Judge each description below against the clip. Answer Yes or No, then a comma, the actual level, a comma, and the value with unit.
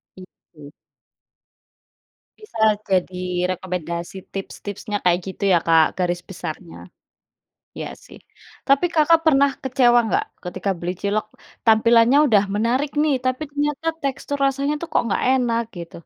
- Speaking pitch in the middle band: No, high, 225 Hz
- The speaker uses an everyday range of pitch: No, wide, 7.2 semitones